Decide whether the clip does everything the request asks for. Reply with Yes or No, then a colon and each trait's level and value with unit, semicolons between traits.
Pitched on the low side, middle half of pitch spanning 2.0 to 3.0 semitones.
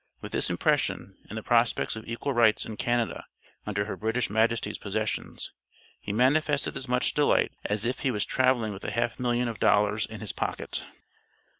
Yes: low, 115 Hz; average, 2.7 semitones